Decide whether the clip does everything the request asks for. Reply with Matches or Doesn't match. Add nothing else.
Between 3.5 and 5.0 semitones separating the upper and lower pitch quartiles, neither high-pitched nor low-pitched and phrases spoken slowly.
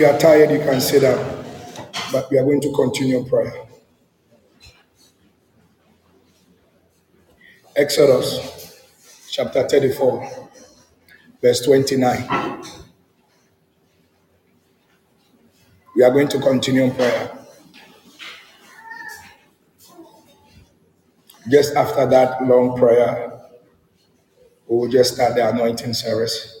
Doesn't match